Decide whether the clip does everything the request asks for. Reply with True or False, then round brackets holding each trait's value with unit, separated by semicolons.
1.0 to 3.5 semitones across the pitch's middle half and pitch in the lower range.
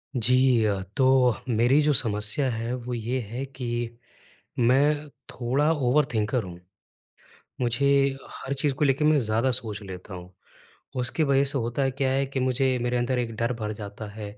True (3.2 semitones; 125 Hz)